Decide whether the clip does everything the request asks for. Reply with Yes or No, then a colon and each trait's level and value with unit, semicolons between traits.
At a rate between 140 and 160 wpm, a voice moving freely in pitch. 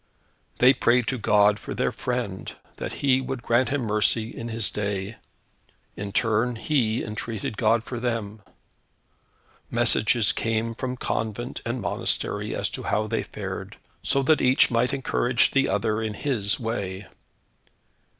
No: average, 145 wpm; average, 2.7 semitones